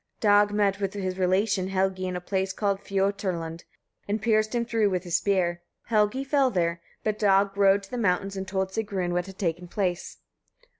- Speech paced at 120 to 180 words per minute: No, average, 190 wpm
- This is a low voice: No, high, 195 Hz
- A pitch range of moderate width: No, narrow, 2.0 semitones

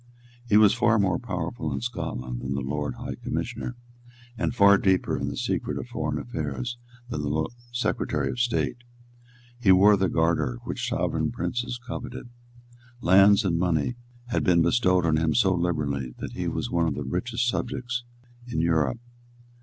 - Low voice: Yes, very low, 90 Hz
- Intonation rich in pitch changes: Yes, wide, 7.1 semitones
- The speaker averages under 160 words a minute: No, average, 165 wpm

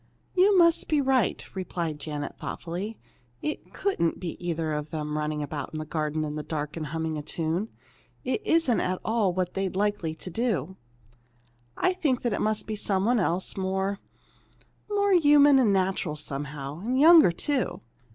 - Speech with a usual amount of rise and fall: No, wide, 7.9 semitones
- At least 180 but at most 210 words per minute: No, average, 170 wpm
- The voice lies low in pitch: No, medium, 185 Hz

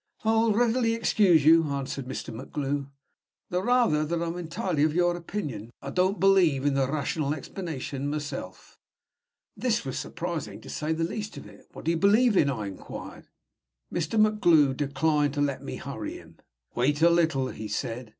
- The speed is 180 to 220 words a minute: No, average, 170 wpm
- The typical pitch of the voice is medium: Yes, medium, 155 Hz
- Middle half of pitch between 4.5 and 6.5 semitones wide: Yes, average, 4.8 semitones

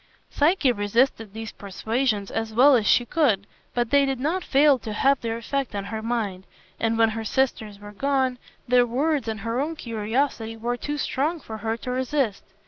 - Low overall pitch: No, high, 240 Hz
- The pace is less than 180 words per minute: No, average, 190 wpm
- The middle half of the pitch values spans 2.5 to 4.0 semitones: Yes, average, 3.7 semitones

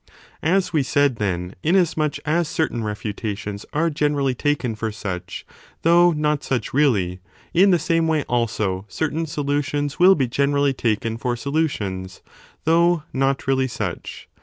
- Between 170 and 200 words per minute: No, average, 150 wpm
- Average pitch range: No, wide, 6.0 semitones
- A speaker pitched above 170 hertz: No, medium, 140 Hz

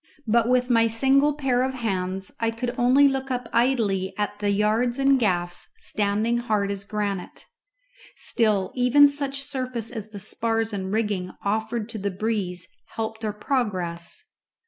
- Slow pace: No, average, 155 wpm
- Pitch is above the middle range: Yes, high, 225 Hz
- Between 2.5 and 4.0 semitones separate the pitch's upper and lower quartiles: Yes, average, 3.6 semitones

